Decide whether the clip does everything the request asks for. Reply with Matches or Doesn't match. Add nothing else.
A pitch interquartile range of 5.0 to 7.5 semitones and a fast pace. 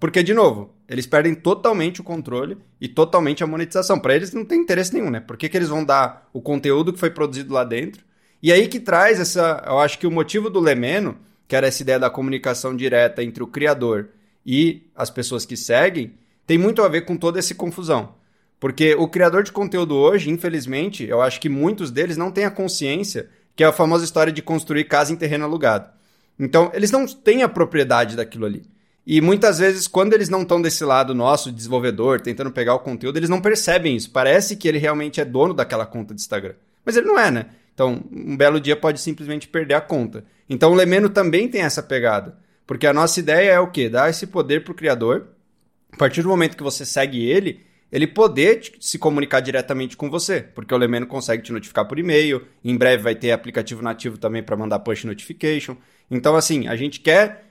Matches